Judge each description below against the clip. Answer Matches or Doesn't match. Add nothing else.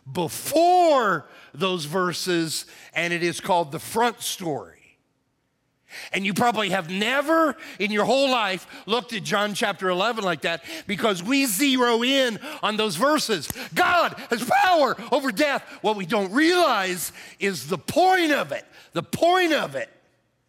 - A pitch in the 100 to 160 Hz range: Doesn't match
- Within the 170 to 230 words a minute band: Doesn't match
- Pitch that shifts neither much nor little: Doesn't match